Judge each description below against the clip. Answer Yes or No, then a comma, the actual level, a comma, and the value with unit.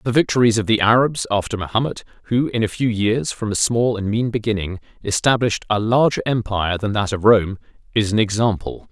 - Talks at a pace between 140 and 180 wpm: No, average, 195 wpm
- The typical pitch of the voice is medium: No, low, 110 Hz